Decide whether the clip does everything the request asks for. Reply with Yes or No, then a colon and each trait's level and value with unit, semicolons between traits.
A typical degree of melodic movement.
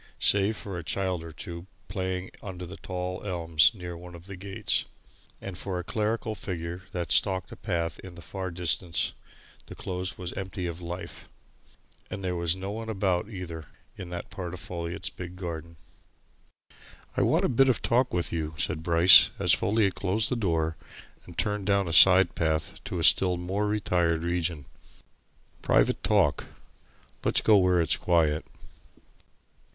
No: narrow, 2.3 semitones